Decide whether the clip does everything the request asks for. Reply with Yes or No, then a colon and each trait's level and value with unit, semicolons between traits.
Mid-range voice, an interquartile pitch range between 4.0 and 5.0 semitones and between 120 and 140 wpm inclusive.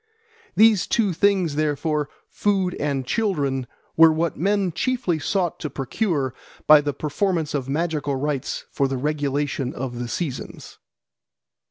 Yes: medium, 150 Hz; average, 4.6 semitones; slow, 135 wpm